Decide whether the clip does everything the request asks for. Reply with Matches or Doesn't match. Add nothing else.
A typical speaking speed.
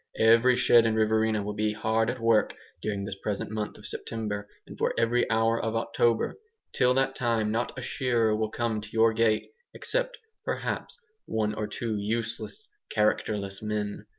Matches